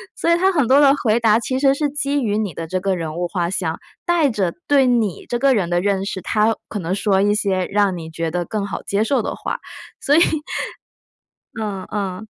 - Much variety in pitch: Yes, wide, 5.8 semitones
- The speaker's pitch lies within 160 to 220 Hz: Yes, high, 205 Hz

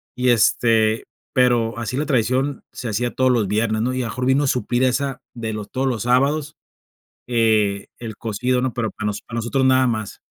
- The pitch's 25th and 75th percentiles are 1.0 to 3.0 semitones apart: Yes, narrow, 2.6 semitones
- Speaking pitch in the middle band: No, low, 120 Hz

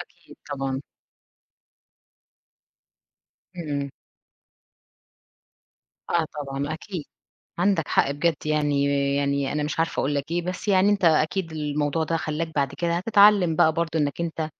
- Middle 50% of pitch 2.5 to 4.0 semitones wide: Yes, average, 3.0 semitones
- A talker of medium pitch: Yes, medium, 155 Hz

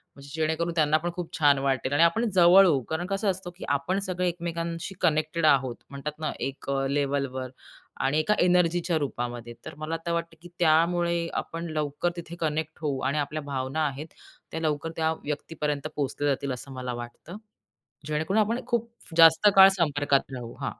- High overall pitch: No, medium, 155 Hz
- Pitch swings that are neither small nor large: Yes, average, 3.4 semitones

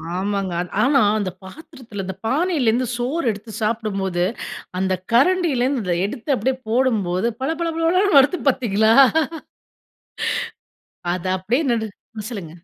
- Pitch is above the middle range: Yes, high, 230 Hz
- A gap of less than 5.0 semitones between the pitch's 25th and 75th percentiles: No, wide, 5.5 semitones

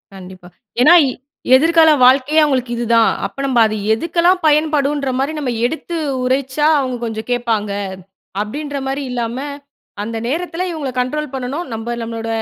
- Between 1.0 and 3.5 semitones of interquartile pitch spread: No, average, 4.4 semitones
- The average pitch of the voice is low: No, very high, 265 Hz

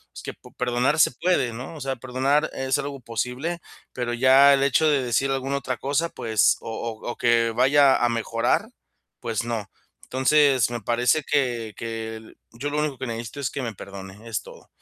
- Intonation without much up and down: No, average, 3.2 semitones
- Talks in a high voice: No, low, 125 Hz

